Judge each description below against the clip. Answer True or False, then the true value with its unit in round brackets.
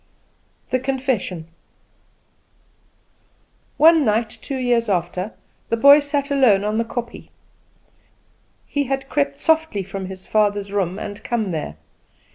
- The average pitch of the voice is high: True (230 Hz)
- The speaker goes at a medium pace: False (120 wpm)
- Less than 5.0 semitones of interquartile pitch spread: False (5.5 semitones)